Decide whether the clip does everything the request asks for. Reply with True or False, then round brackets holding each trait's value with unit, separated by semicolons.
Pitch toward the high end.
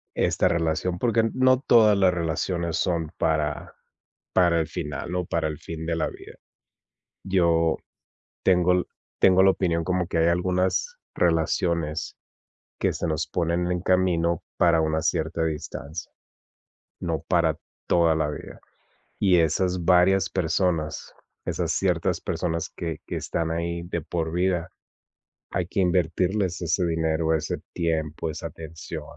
False (85 Hz)